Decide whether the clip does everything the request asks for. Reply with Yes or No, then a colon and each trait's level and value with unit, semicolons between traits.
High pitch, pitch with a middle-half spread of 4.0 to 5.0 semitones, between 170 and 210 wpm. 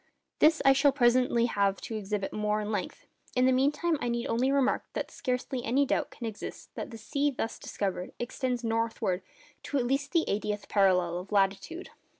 Yes: high, 235 Hz; average, 4.6 semitones; average, 185 wpm